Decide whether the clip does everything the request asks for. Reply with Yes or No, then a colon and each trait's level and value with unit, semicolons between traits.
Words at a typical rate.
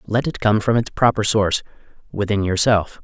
Yes: average, 160 wpm